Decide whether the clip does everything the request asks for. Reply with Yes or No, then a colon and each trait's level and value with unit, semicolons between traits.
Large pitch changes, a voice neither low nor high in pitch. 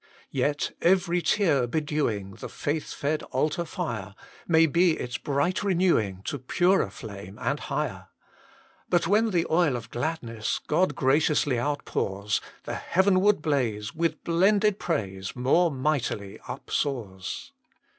Yes: wide, 6.6 semitones; medium, 145 Hz